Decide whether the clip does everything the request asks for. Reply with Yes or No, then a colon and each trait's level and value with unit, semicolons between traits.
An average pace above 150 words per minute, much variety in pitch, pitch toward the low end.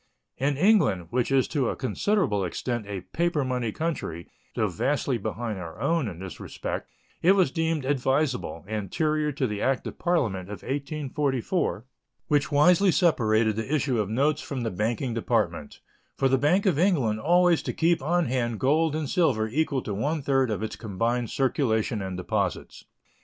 Yes: average, 170 wpm; wide, 5.9 semitones; low, 130 Hz